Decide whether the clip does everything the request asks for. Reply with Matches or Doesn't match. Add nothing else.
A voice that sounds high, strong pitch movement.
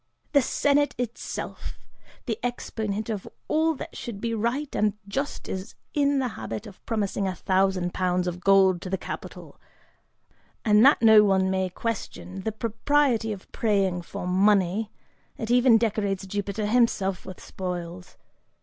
Doesn't match